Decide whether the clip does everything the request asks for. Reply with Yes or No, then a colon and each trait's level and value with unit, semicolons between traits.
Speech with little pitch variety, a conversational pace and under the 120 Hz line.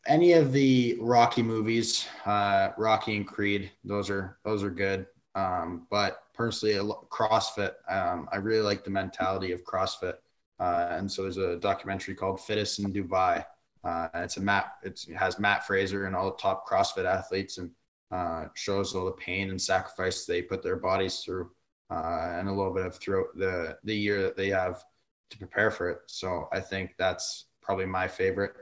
Yes: narrow, 2.0 semitones; average, 185 wpm; low, 100 Hz